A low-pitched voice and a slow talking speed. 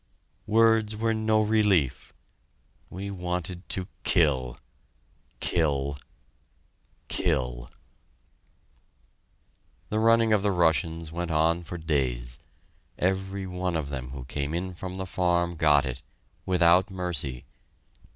Yes: very low, 85 Hz; slow, 110 wpm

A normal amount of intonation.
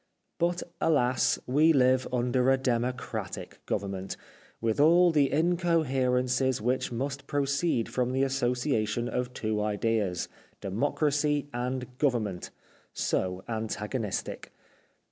Yes: average, 3.7 semitones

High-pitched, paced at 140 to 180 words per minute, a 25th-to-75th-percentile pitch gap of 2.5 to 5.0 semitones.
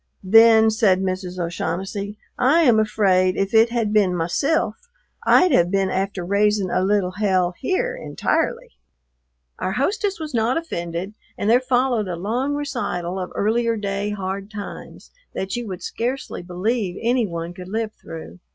Yes: high, 205 Hz; average, 155 wpm; average, 4.5 semitones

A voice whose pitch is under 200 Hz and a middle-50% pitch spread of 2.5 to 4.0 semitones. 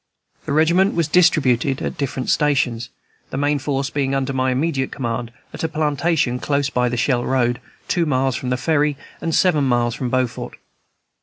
Yes: low, 135 Hz; average, 3.1 semitones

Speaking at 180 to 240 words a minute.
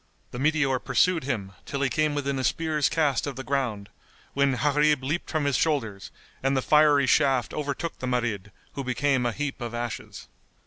Yes: average, 185 wpm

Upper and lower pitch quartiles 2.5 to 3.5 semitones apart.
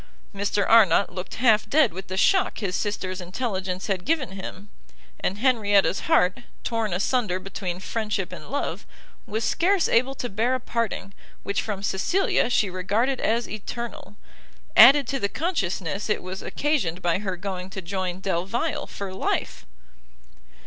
No: average, 4.1 semitones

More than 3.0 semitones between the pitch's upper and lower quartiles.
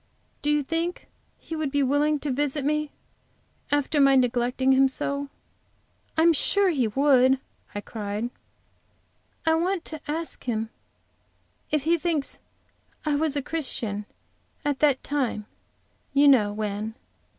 Yes: average, 3.4 semitones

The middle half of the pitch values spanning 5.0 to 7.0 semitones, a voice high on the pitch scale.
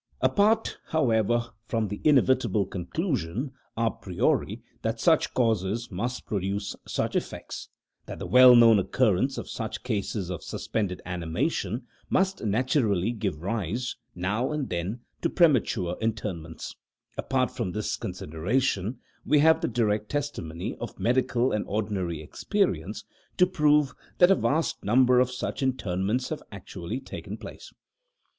No: average, 5.3 semitones; low, 115 Hz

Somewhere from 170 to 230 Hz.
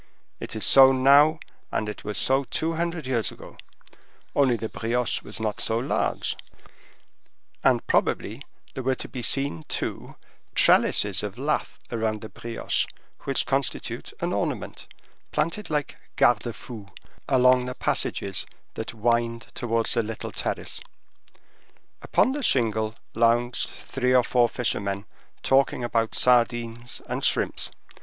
No: low, 120 Hz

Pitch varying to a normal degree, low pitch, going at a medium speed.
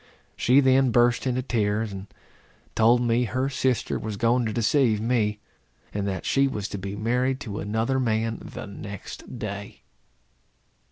Yes: average, 3.4 semitones; low, 115 Hz; average, 155 wpm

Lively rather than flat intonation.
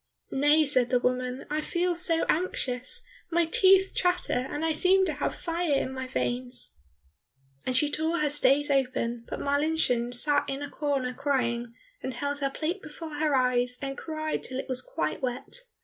No: average, 4.0 semitones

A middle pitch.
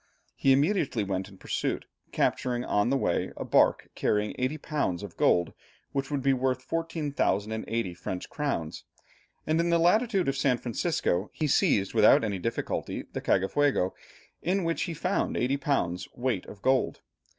No: low, 130 Hz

